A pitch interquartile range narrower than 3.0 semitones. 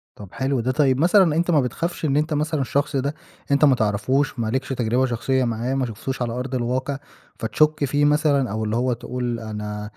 No: average, 3.4 semitones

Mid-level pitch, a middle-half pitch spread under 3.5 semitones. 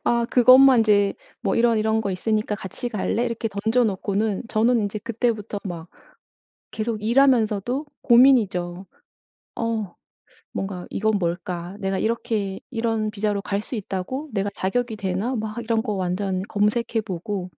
No: high, 215 Hz; average, 3.0 semitones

